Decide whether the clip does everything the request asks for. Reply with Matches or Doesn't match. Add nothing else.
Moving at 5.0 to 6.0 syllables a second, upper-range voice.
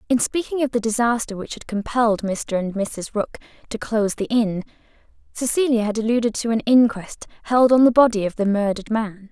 Matches